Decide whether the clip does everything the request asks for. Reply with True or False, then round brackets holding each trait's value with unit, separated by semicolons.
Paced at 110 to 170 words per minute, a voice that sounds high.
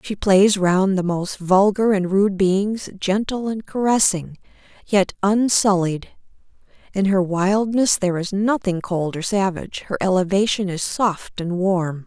True (145 wpm; 195 Hz)